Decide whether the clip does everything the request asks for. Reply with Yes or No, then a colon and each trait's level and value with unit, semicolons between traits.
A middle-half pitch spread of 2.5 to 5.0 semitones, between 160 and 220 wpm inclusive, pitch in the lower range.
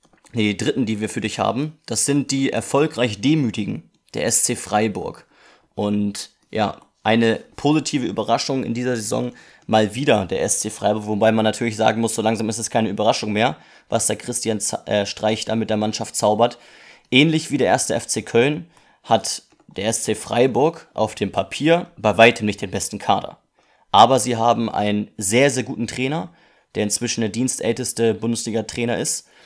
Yes: average, 2.9 semitones; average, 175 wpm; low, 115 Hz